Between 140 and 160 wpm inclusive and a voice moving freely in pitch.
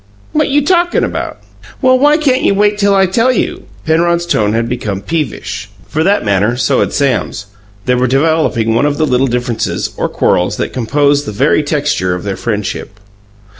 No: average, 185 wpm; wide, 9.0 semitones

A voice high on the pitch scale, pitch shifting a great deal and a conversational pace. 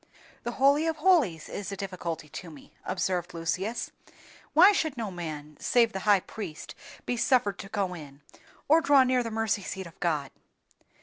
Yes: high, 200 Hz; wide, 6.6 semitones; average, 175 wpm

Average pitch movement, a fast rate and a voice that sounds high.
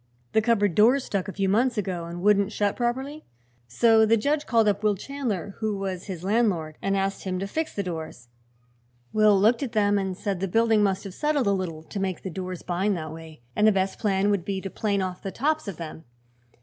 Yes: average, 3.0 semitones; fast, 225 wpm; high, 200 Hz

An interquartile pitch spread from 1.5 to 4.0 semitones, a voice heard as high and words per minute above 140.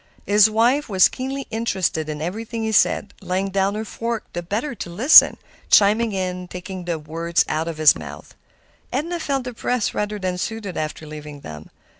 No: average, 5.0 semitones; high, 195 Hz; average, 175 wpm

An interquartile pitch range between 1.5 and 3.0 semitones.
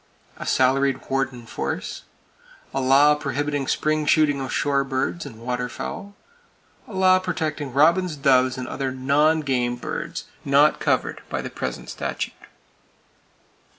Yes: narrow, 2.6 semitones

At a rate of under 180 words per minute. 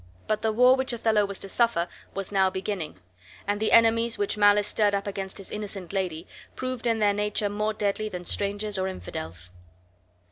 No: average, 185 wpm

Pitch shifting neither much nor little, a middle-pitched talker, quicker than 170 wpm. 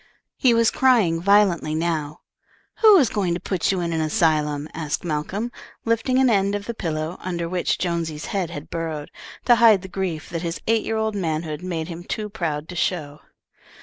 Yes: average, 4.8 semitones; medium, 175 Hz; average, 190 wpm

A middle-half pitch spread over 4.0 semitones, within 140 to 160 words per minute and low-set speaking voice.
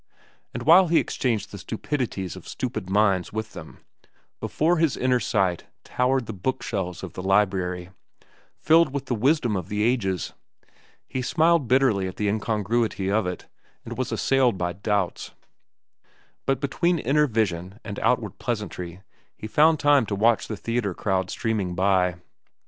Yes: wide, 5.5 semitones; average, 155 wpm; low, 110 Hz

